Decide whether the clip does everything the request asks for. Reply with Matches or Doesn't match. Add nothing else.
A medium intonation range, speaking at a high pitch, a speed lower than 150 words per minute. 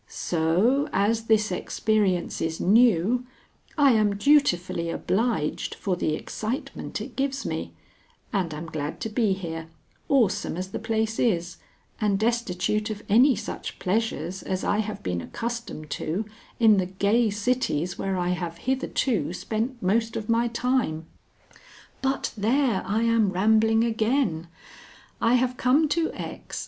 Matches